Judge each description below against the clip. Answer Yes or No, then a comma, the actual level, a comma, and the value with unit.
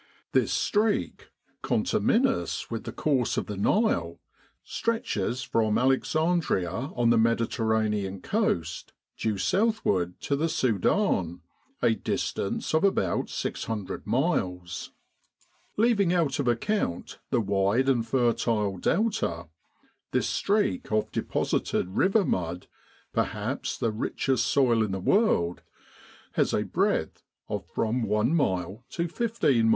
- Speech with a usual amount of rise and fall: No, wide, 8.6 semitones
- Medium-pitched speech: No, low, 115 Hz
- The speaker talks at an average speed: No, slow, 120 wpm